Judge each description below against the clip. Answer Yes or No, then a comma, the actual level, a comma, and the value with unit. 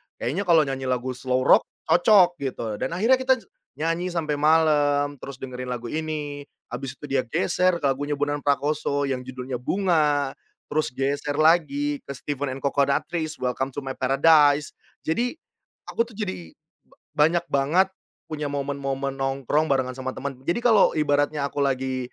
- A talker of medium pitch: Yes, medium, 145 Hz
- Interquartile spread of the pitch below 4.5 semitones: Yes, average, 2.9 semitones